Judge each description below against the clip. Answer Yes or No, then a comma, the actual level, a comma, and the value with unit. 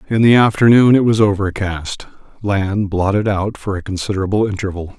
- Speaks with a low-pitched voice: Yes, low, 100 Hz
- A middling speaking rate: Yes, average, 155 wpm